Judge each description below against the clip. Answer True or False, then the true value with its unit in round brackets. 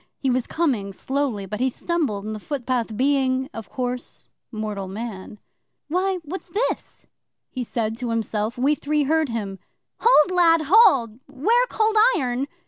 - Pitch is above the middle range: True (255 Hz)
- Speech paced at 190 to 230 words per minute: False (150 wpm)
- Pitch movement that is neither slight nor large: False (5.8 semitones)